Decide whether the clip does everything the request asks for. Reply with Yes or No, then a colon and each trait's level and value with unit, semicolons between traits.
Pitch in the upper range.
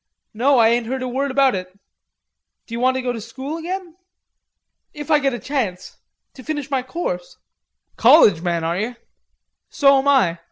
Yes: very high, 255 Hz